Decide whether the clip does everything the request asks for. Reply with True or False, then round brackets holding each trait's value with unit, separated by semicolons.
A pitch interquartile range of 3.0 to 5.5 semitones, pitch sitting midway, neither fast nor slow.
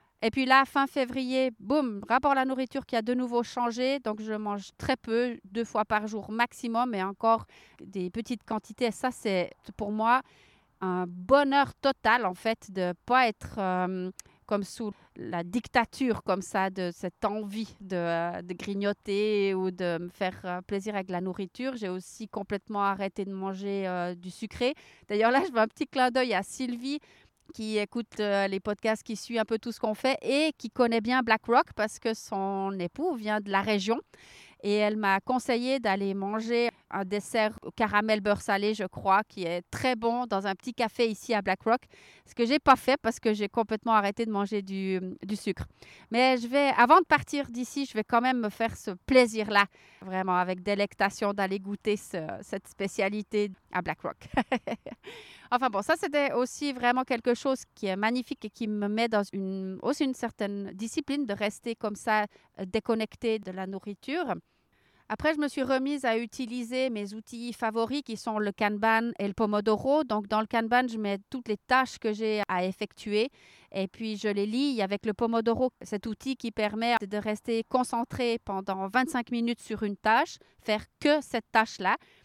False (3.6 semitones; 220 Hz; 190 wpm)